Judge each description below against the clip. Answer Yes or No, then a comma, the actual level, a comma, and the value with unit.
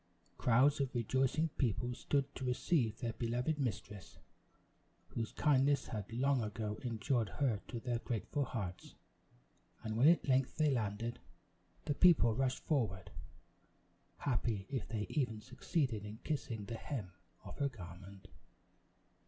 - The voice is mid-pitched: No, low, 120 Hz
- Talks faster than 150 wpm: No, slow, 135 wpm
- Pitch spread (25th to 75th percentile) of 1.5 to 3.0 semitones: No, average, 4.0 semitones